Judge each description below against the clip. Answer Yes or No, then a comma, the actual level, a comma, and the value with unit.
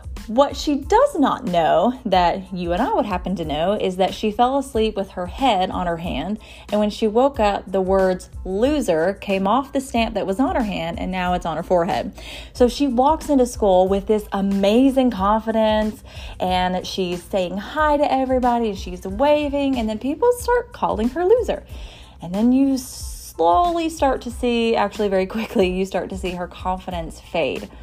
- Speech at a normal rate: Yes, average, 190 wpm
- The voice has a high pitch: Yes, high, 215 Hz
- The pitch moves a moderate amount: No, wide, 5.9 semitones